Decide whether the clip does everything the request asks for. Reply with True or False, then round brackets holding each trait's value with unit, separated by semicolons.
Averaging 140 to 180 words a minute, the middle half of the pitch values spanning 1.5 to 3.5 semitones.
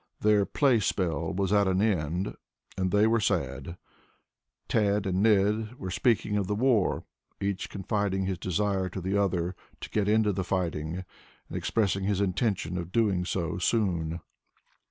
True (155 wpm; 2.4 semitones)